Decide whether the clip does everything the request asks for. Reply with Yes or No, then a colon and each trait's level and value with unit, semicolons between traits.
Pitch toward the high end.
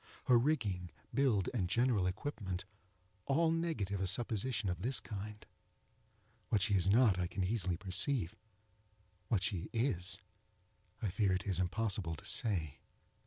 No: low, 100 Hz